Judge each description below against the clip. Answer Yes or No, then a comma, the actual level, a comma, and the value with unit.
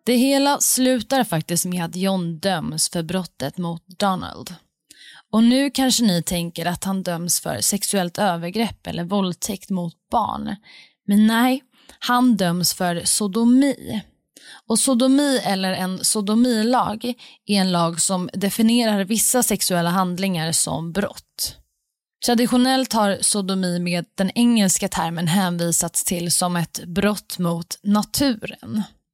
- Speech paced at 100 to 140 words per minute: Yes, average, 130 wpm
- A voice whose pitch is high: Yes, high, 195 Hz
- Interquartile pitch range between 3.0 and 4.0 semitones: No, average, 4.9 semitones